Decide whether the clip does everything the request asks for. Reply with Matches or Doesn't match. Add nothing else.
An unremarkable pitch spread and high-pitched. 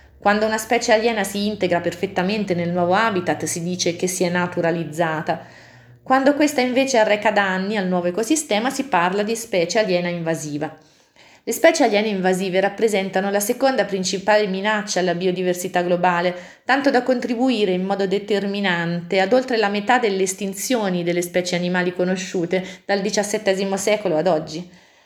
Matches